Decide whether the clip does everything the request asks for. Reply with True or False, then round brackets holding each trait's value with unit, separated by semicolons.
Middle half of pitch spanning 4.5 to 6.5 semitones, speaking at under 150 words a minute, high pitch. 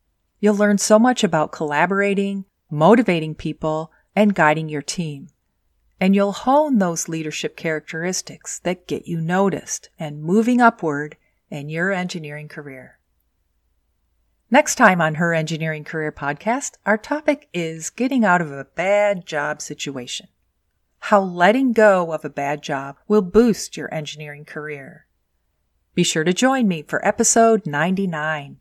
False (5.1 semitones; 140 wpm; 160 Hz)